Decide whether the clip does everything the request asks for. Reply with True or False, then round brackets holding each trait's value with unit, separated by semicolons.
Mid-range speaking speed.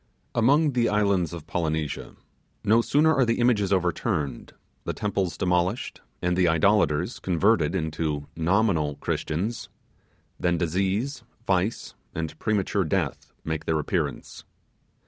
False (120 wpm)